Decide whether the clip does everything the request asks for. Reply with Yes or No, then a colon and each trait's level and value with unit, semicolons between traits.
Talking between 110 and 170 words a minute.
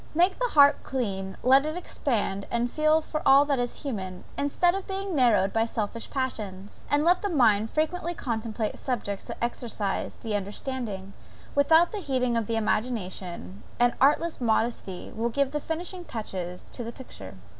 Yes: average, 160 wpm